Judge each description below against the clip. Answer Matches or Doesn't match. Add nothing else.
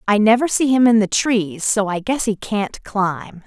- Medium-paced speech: Doesn't match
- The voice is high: Matches